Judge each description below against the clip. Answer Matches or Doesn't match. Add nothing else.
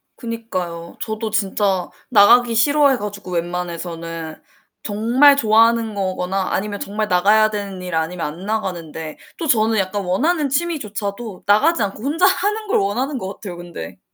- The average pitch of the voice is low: Doesn't match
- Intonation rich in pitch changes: Doesn't match